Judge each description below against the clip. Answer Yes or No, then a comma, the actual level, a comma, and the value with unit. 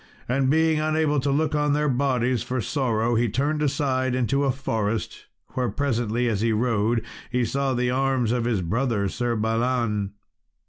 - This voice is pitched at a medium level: No, low, 125 Hz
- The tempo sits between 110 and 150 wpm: No, average, 170 wpm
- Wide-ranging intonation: No, average, 3.2 semitones